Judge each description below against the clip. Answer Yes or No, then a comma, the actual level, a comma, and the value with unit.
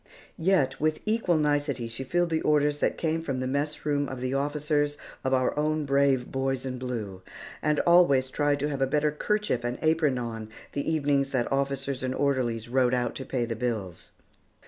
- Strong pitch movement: No, average, 2.7 semitones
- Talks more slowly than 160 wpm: No, average, 190 wpm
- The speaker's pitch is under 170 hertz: Yes, medium, 140 Hz